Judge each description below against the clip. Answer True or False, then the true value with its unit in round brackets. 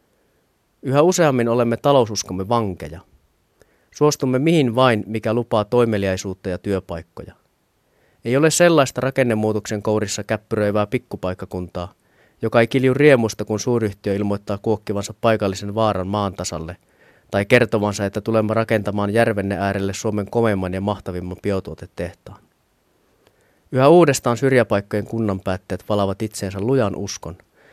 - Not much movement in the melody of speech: False (3.2 semitones)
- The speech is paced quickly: False (115 wpm)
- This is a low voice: True (105 Hz)